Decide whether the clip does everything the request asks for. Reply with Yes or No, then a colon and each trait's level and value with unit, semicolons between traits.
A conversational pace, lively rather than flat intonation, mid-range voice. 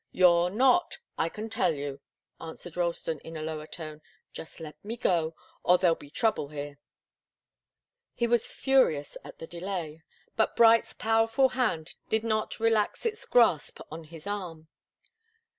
Yes: average, 150 wpm; wide, 6.0 semitones; medium, 175 Hz